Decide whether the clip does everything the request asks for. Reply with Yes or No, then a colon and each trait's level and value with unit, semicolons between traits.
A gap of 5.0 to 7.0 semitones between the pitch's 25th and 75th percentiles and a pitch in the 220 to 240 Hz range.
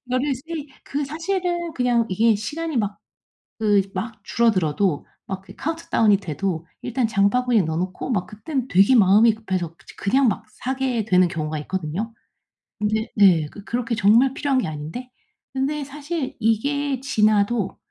Yes: wide, 5.5 semitones; high, 225 Hz